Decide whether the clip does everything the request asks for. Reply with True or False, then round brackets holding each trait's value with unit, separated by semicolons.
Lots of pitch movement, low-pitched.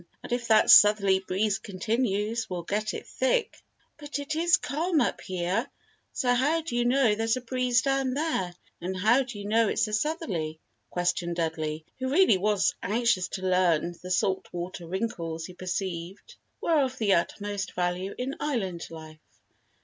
False (5.8 semitones; 210 Hz)